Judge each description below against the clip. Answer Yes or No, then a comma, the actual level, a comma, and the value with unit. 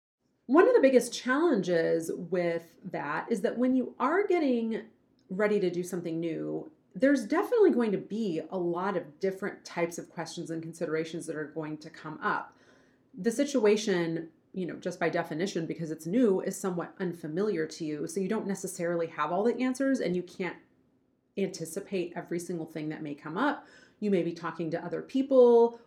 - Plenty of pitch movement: Yes, wide, 5.9 semitones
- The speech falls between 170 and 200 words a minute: Yes, average, 185 wpm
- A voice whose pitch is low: No, medium, 185 Hz